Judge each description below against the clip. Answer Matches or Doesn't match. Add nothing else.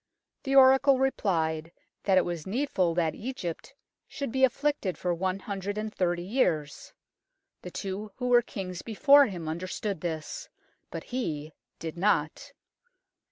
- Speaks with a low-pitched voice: Doesn't match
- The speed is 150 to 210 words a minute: Doesn't match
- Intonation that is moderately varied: Doesn't match